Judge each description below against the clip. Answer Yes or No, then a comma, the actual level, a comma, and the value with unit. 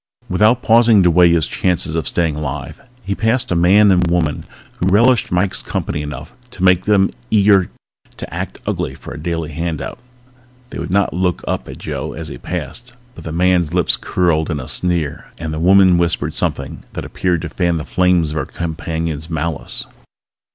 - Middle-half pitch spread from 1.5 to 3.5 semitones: Yes, average, 2.9 semitones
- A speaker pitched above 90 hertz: No, very low, 85 Hz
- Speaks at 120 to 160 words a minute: No, average, 190 wpm